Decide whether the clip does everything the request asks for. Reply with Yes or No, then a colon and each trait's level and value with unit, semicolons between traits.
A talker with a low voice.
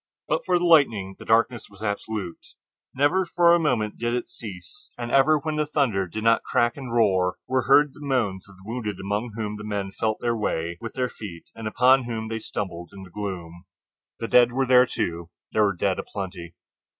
Yes: low, 110 Hz